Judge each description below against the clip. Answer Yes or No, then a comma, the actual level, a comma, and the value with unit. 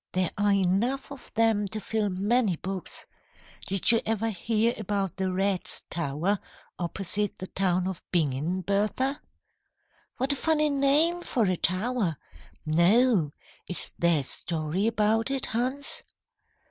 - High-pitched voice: Yes, high, 200 Hz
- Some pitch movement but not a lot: Yes, average, 4.5 semitones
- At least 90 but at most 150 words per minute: Yes, slow, 135 wpm